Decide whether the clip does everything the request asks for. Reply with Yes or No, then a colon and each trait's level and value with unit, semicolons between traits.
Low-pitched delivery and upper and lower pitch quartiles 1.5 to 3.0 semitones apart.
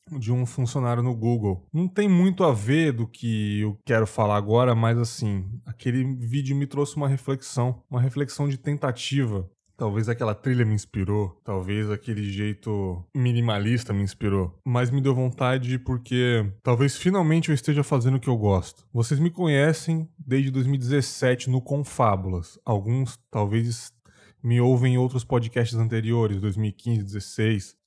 No: low, 120 Hz; average, 4.1 semitones